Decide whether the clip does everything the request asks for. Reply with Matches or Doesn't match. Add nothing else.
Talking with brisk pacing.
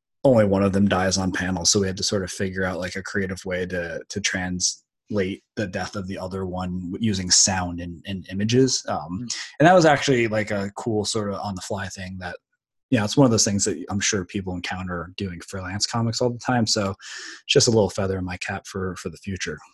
Matches